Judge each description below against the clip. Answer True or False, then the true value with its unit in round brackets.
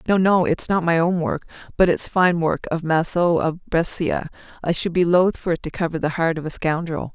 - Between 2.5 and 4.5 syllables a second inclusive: False (5.0 syllables/s)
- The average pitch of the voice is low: False (170 Hz)